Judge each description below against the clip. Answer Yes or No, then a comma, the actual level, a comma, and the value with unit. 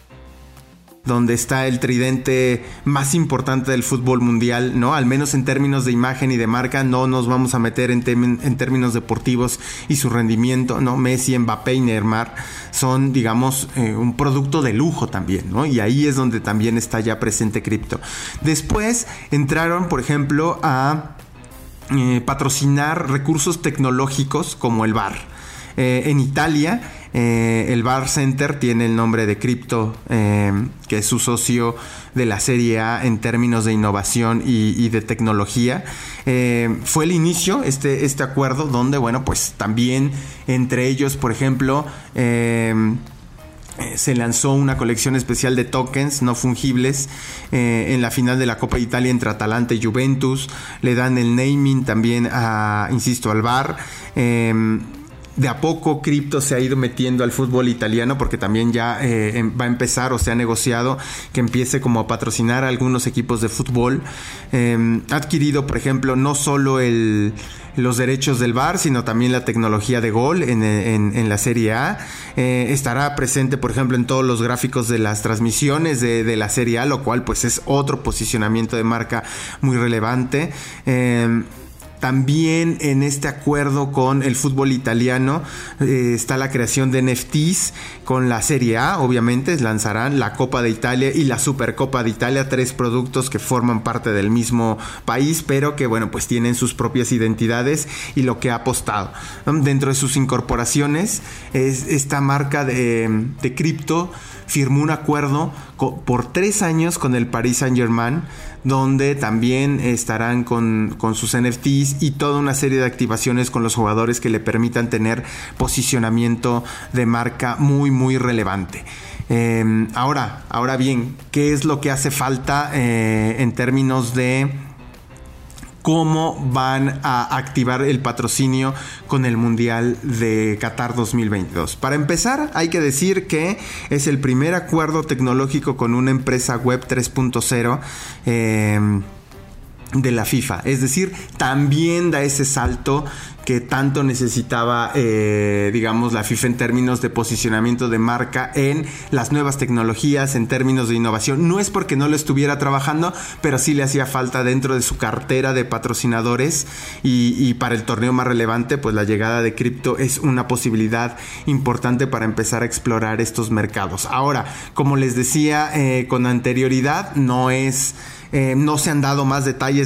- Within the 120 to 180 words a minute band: Yes, average, 160 wpm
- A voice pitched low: Yes, low, 125 Hz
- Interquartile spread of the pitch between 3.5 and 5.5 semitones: No, average, 2.8 semitones